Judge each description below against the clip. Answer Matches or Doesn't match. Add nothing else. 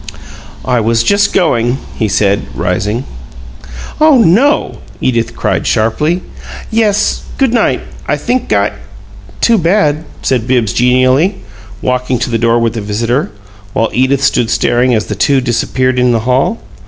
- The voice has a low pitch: Matches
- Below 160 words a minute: Matches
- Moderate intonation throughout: Doesn't match